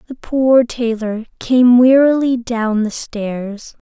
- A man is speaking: No, female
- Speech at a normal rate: No, slow, 125 wpm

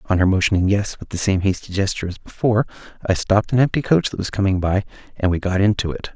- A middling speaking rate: No, fast, 245 wpm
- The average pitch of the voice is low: Yes, low, 100 Hz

